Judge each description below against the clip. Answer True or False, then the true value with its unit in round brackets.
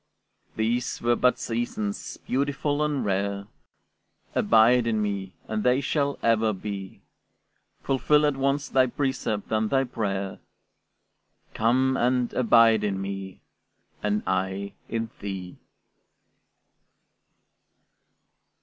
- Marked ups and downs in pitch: False (4.4 semitones)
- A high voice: False (115 Hz)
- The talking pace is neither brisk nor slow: False (105 wpm)